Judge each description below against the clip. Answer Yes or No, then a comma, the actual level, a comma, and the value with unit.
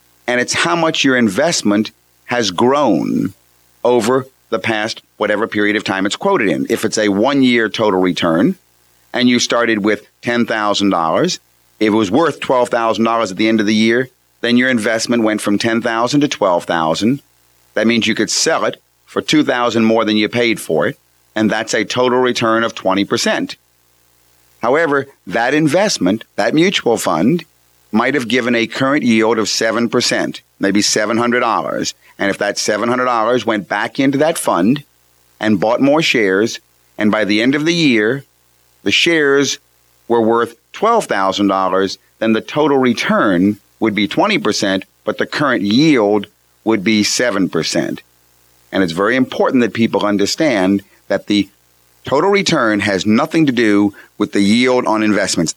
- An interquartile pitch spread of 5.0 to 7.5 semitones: No, average, 4.0 semitones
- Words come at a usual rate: Yes, average, 155 wpm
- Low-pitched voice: Yes, low, 110 Hz